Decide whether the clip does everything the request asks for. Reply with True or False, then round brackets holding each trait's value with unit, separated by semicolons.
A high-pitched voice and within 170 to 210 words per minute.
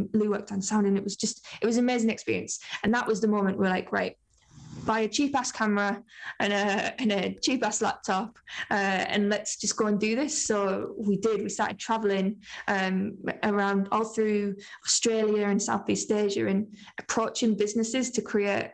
True (210 Hz; 185 wpm)